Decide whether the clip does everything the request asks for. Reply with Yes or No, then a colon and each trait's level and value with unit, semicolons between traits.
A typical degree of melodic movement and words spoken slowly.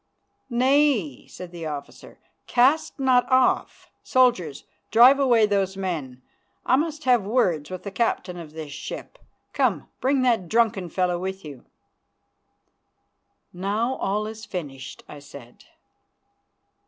No: wide, 7.0 semitones; slow, 125 wpm